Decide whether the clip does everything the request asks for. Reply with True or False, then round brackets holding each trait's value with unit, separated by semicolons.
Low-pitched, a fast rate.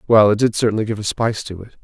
True (110 Hz; 295 wpm)